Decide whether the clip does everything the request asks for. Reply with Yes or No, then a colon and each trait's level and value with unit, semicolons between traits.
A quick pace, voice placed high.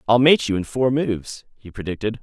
No: fast, 215 wpm; low, 115 Hz